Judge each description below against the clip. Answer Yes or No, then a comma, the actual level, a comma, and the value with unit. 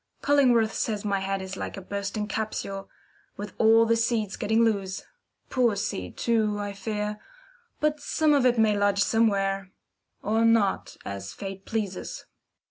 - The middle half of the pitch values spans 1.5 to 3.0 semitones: Yes, narrow, 2.6 semitones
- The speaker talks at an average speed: Yes, average, 150 wpm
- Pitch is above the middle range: Yes, high, 210 Hz